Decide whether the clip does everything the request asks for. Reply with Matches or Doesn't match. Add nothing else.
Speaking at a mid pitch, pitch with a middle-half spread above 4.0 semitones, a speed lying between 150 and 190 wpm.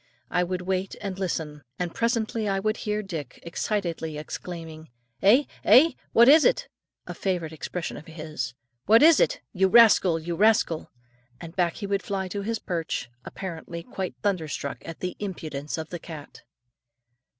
Matches